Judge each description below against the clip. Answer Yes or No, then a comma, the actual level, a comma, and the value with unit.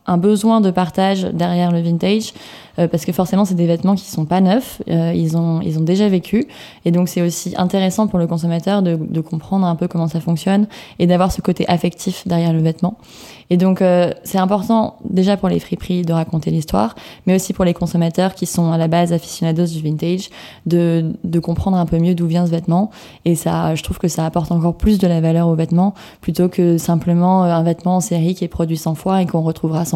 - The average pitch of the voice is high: No, medium, 175 Hz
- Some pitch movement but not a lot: No, narrow, 1.9 semitones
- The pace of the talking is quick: Yes, fast, 230 wpm